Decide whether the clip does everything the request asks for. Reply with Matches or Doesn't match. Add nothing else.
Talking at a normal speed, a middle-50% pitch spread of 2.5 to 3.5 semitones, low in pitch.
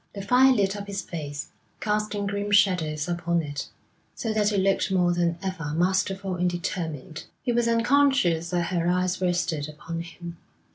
Doesn't match